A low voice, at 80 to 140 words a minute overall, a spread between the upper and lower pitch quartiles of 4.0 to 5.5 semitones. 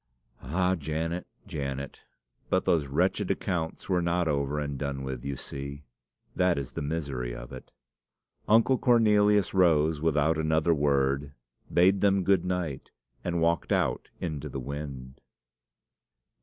Yes: very low, 80 Hz; slow, 135 wpm; average, 4.3 semitones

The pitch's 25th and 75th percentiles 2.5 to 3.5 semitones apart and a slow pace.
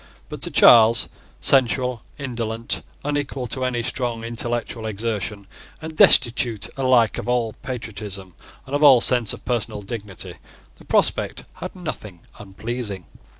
Yes: average, 2.9 semitones; slow, 130 wpm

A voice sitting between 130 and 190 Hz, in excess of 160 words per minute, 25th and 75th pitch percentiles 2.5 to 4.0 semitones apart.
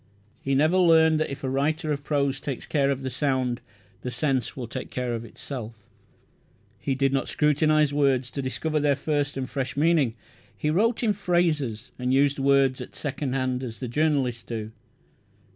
Yes: medium, 140 Hz; average, 180 wpm; average, 2.9 semitones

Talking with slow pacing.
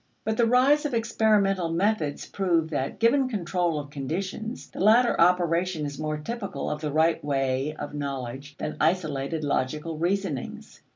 No: average, 155 wpm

